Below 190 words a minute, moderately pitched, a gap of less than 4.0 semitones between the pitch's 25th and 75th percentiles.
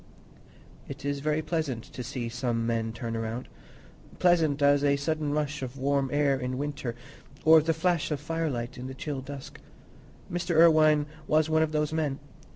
Yes: average, 170 wpm; medium, 145 Hz; average, 3.2 semitones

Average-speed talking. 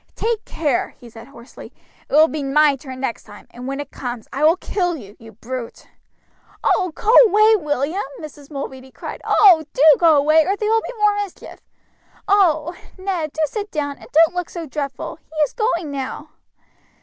Yes: average, 185 wpm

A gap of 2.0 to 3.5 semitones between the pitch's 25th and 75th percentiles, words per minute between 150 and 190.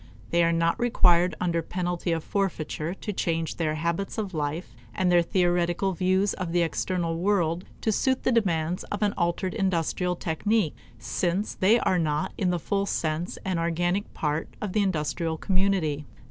Yes: narrow, 2.6 semitones; average, 170 wpm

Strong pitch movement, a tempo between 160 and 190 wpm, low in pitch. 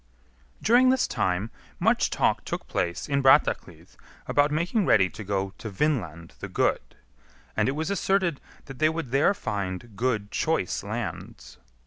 No: wide, 8.2 semitones; average, 150 wpm; low, 120 Hz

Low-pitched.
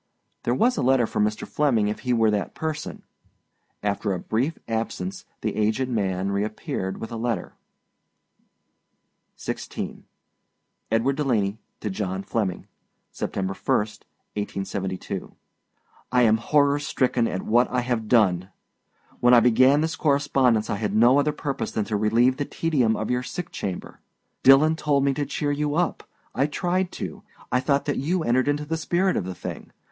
Yes: low, 120 Hz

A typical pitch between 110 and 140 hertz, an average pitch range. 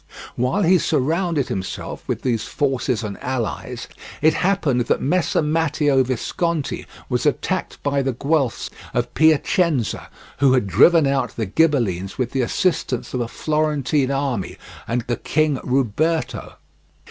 Yes: low, 135 Hz; average, 4.1 semitones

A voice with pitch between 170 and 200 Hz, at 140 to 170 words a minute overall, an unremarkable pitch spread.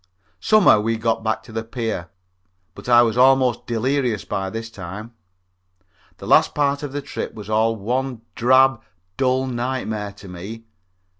No: low, 115 Hz; average, 155 wpm; average, 3.1 semitones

